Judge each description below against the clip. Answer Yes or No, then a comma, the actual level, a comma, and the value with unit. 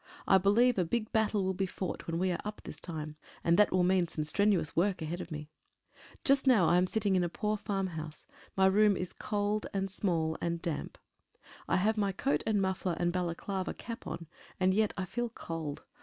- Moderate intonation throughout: Yes, average, 3.4 semitones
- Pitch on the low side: No, high, 190 Hz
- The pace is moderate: No, fast, 210 wpm